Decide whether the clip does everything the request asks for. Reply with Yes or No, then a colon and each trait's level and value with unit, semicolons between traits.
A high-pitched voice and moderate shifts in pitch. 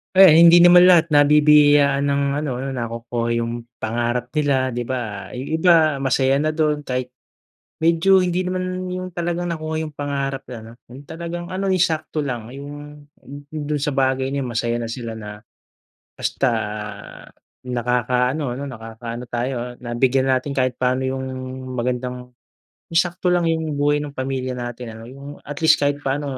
No: low, 135 Hz; average, 4.1 semitones